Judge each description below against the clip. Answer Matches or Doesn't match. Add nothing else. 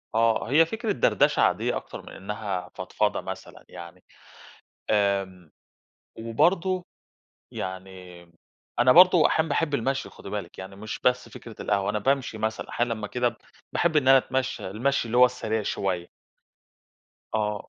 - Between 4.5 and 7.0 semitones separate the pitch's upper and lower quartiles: Matches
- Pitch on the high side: Doesn't match